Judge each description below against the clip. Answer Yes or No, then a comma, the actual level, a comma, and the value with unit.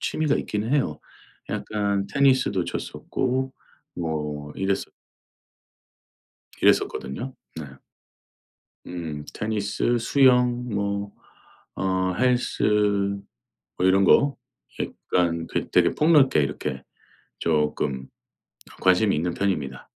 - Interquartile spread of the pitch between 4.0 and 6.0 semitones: No, wide, 6.7 semitones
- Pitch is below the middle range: Yes, low, 100 Hz